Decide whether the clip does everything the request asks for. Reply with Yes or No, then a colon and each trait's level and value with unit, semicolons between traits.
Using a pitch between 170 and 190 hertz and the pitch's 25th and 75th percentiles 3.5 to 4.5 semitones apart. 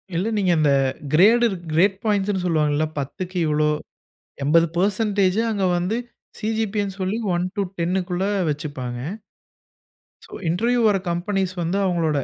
Yes: medium, 185 Hz; average, 3.8 semitones